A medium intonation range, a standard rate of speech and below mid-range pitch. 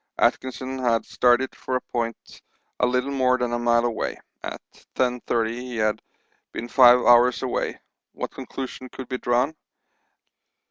No: narrow, 1.3 semitones; average, 145 wpm; low, 125 Hz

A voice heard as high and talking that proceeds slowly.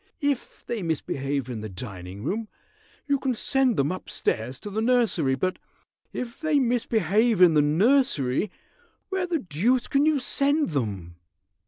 No: high, 200 Hz; average, 155 wpm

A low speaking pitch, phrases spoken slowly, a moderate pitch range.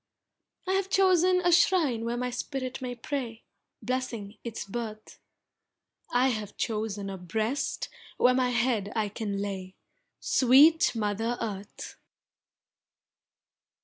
No: high, 235 Hz; slow, 115 wpm; average, 3.7 semitones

